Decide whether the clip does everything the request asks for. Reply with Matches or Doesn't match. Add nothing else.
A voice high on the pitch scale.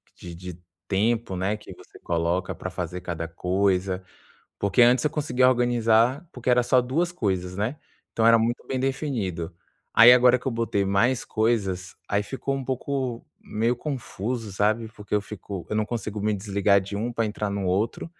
Doesn't match